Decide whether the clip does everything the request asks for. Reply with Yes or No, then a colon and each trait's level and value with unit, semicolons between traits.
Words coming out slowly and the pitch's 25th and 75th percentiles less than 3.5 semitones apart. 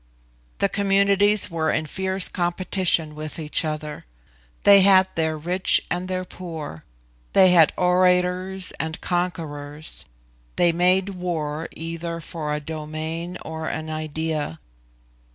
Yes: slow, 120 wpm; average, 2.7 semitones